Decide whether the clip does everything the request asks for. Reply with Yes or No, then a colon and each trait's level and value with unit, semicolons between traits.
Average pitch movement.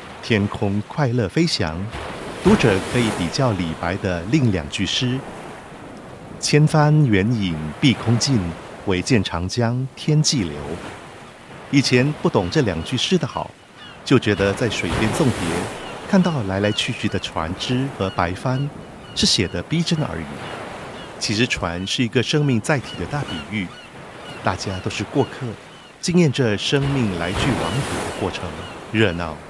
No: wide, 6.3 semitones